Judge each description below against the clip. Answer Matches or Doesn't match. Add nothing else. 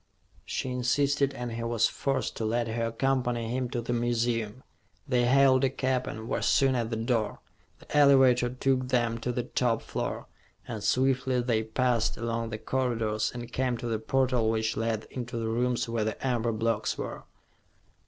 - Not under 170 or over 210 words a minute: Matches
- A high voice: Doesn't match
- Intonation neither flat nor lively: Doesn't match